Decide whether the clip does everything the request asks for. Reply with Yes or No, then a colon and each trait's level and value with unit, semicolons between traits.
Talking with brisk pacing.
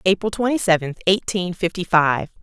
No: average, 150 wpm